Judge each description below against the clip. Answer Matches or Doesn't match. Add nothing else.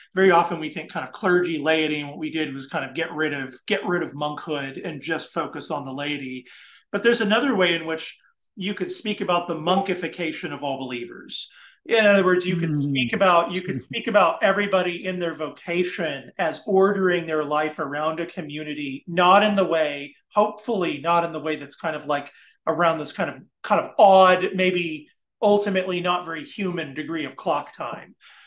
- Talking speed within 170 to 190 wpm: Doesn't match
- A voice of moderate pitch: Matches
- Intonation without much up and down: Doesn't match